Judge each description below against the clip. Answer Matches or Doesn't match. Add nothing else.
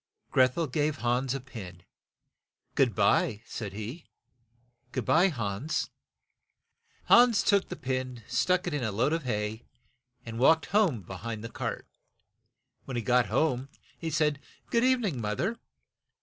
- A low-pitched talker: Matches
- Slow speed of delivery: Doesn't match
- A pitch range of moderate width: Doesn't match